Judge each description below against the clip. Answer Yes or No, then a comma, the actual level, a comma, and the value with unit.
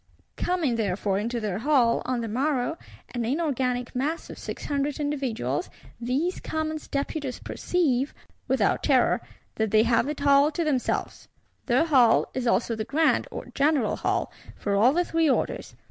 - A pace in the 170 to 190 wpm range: No, average, 160 wpm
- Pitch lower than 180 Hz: No, very high, 260 Hz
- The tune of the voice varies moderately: Yes, average, 4.5 semitones